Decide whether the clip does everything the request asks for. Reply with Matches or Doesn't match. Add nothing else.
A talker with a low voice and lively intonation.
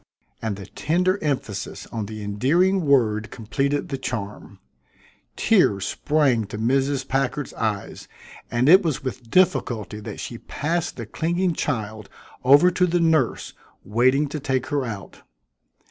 Matches